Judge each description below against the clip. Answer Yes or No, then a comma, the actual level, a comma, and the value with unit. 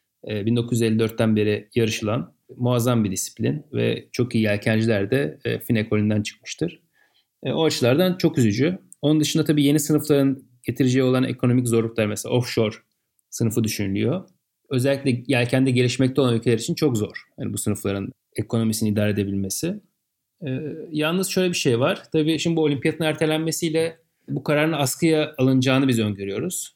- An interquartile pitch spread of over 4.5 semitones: Yes, wide, 5.4 semitones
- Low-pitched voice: Yes, low, 130 Hz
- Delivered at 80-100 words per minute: No, average, 135 wpm